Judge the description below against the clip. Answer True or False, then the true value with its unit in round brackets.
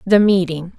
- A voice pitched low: False (185 Hz)